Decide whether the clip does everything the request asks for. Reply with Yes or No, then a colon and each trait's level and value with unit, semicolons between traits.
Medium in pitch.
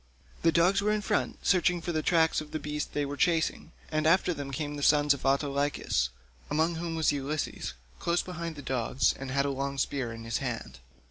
Yes: medium, 150 Hz